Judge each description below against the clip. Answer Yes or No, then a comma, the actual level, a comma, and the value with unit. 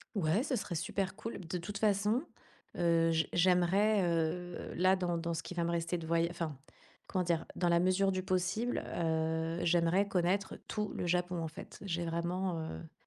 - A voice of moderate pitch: Yes, medium, 175 Hz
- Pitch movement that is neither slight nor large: No, narrow, 2.3 semitones